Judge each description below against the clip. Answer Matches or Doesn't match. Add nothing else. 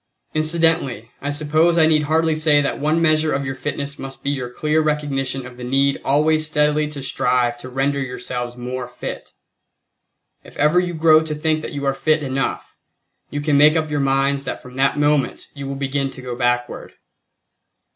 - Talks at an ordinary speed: Matches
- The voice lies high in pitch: Doesn't match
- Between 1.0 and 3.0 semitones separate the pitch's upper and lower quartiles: Matches